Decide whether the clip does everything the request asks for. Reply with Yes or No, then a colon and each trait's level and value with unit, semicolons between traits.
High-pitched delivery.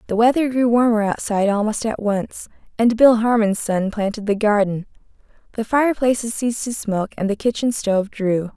Yes: high, 220 Hz